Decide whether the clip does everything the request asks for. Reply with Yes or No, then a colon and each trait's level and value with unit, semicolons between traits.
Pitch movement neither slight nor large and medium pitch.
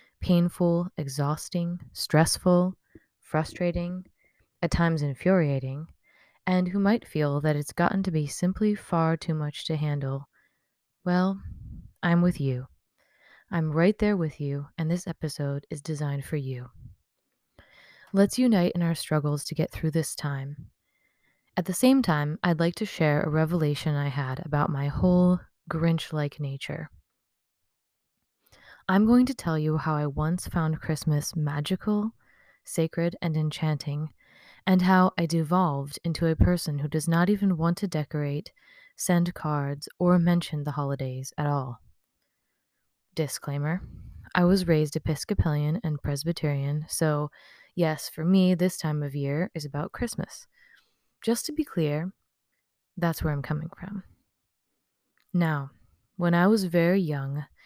Yes: average, 3.3 semitones; medium, 160 Hz